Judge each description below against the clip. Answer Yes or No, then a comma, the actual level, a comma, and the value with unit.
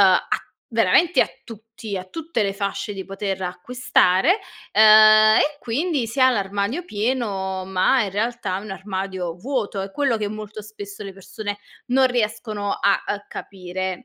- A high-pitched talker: Yes, high, 205 Hz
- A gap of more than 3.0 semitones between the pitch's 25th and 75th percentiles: Yes, average, 3.7 semitones